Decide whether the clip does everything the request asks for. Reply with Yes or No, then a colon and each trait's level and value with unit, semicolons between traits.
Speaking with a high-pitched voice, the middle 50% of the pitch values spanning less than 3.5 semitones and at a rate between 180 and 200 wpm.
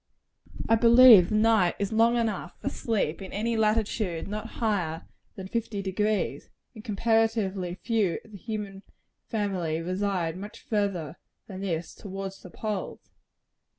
No: high, 205 Hz; average, 3.0 semitones; average, 140 wpm